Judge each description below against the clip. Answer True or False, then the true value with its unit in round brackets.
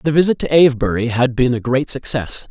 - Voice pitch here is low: True (130 Hz)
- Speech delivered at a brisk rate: True (215 wpm)